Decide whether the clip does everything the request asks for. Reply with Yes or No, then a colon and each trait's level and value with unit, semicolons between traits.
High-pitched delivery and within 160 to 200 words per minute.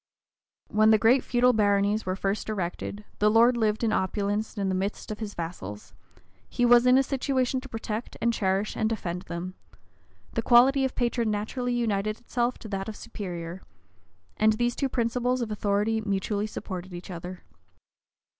Yes: high, 215 Hz; average, 170 wpm